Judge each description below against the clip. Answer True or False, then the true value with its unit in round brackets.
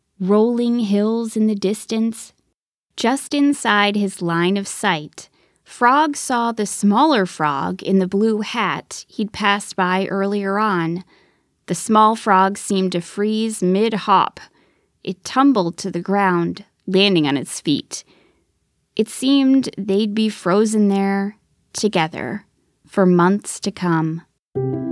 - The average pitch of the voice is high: True (200 Hz)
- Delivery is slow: True (130 wpm)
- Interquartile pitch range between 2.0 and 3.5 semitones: True (2.9 semitones)